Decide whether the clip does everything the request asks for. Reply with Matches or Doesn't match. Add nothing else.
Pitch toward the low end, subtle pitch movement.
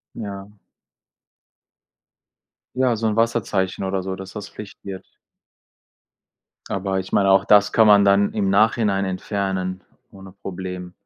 Matches